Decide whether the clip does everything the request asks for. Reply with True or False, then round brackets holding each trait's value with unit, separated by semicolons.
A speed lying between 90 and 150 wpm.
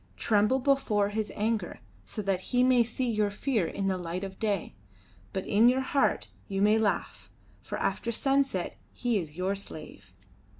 False (170 wpm)